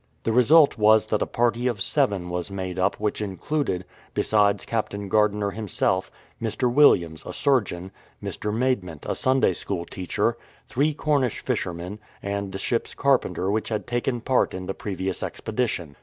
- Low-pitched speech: Yes, low, 105 Hz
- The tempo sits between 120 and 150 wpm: No, average, 160 wpm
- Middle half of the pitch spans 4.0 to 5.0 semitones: Yes, average, 4.6 semitones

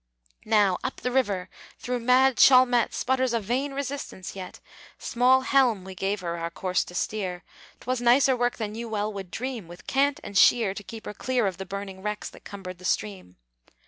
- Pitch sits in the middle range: No, high, 215 Hz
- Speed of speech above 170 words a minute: Yes, average, 195 wpm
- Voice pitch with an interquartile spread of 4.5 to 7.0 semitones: Yes, average, 5.0 semitones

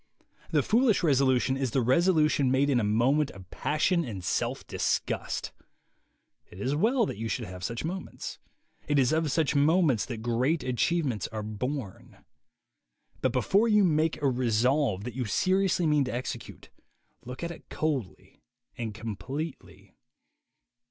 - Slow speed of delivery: No, average, 150 wpm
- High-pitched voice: No, low, 135 Hz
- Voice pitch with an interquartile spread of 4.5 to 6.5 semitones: Yes, average, 5.3 semitones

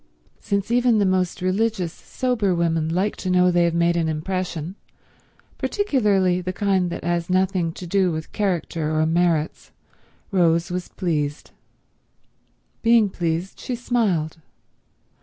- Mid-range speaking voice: Yes, medium, 180 Hz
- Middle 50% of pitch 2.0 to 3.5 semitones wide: Yes, average, 2.9 semitones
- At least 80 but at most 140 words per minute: Yes, slow, 135 wpm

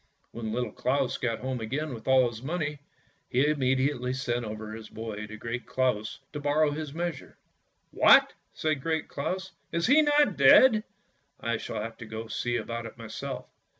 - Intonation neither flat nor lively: Yes, average, 4.8 semitones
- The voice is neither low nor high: No, low, 130 Hz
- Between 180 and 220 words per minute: Yes, average, 190 wpm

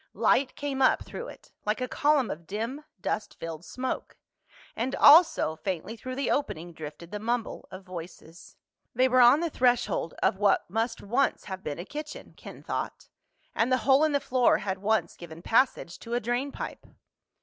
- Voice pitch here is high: Yes, high, 230 Hz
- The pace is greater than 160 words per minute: Yes, average, 185 wpm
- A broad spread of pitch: Yes, wide, 6.0 semitones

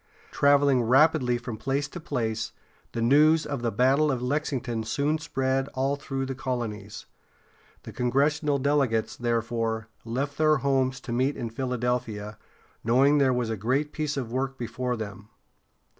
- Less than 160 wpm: Yes, average, 150 wpm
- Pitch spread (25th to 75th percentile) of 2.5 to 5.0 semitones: Yes, average, 3.3 semitones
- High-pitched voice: No, low, 130 Hz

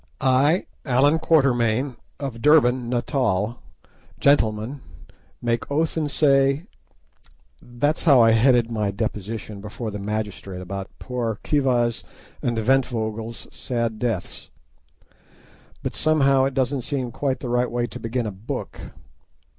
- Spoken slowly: Yes, slow, 120 wpm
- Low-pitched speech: Yes, low, 120 Hz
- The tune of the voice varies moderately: Yes, average, 3.6 semitones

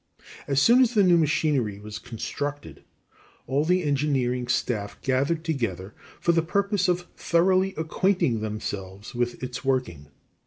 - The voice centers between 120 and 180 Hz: Yes, medium, 140 Hz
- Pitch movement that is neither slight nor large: No, wide, 6.7 semitones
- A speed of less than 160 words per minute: Yes, average, 140 wpm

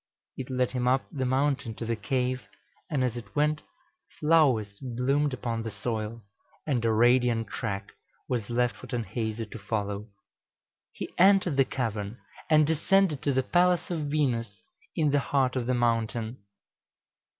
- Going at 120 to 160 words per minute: Yes, average, 155 wpm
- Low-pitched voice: Yes, low, 125 Hz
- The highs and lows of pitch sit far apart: No, average, 3.9 semitones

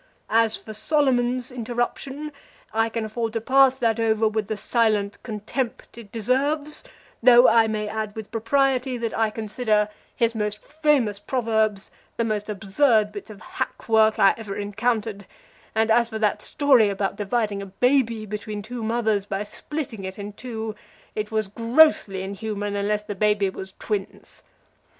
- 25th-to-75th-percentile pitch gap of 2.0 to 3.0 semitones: Yes, narrow, 2.5 semitones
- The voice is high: Yes, high, 220 Hz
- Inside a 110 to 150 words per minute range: No, average, 160 wpm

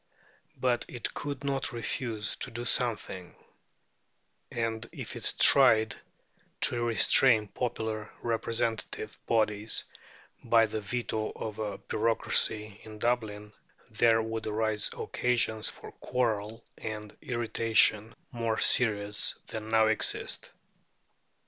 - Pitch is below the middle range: Yes, low, 110 Hz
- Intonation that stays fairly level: Yes, narrow, 1.7 semitones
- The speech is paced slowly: Yes, slow, 105 wpm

